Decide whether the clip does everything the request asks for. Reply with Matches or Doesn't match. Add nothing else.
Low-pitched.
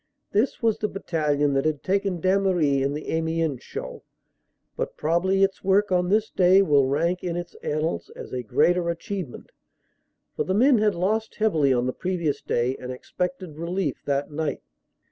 Doesn't match